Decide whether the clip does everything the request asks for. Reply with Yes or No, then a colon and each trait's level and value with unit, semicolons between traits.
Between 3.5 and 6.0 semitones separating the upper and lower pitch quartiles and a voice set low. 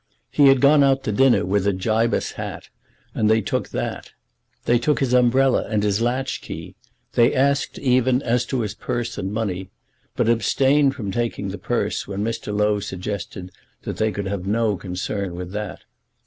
Yes: average, 3.9 semitones; low, 110 Hz